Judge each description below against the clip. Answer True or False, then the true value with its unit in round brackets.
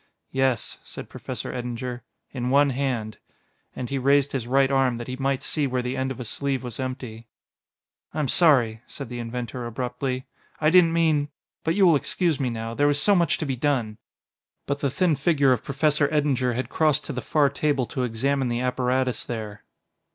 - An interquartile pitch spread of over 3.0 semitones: False (2.7 semitones)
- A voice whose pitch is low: True (130 Hz)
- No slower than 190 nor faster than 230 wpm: True (200 wpm)